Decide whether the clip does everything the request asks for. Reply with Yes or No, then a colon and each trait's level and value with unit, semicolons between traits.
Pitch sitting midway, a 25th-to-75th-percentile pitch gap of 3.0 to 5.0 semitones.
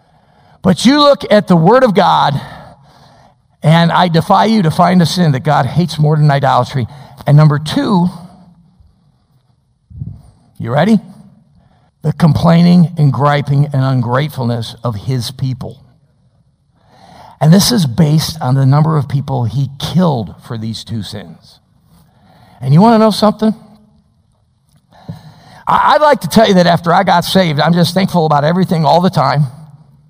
Yes: medium, 155 Hz; average, 4.4 semitones